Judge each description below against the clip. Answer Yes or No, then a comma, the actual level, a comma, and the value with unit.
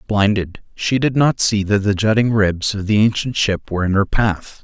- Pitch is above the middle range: No, low, 105 Hz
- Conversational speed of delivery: No, fast, 220 wpm